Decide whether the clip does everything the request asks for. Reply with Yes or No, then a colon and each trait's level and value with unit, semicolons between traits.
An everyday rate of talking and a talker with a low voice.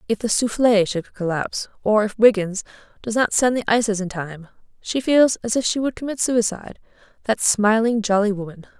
No: average, 170 wpm; high, 215 Hz